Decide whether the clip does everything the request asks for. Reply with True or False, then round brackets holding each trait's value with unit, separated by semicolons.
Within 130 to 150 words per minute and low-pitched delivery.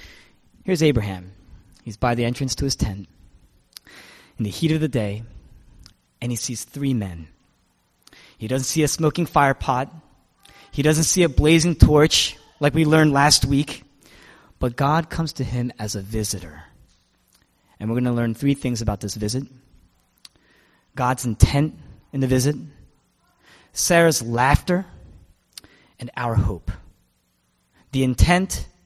True (140 wpm; 120 Hz)